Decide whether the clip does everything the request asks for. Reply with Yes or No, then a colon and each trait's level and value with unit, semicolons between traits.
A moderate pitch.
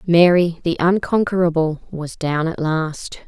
Yes: medium, 165 Hz